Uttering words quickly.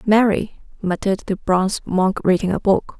No: average, 160 wpm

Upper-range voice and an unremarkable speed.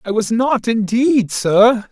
Yes: high, 225 Hz; average, 155 wpm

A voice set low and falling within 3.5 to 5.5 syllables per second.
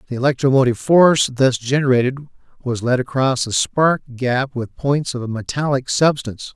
Yes: low, 130 Hz; 5.0 syllables/s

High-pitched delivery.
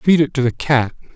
No: low, 135 Hz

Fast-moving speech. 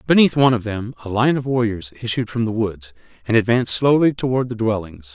Yes: fast, 210 wpm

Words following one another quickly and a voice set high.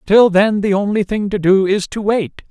Yes: fast, 240 wpm; high, 200 Hz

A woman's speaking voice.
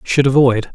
No: male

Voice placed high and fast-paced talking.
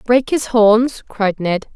No: high, 225 Hz; average, 170 wpm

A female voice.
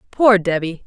Yes: female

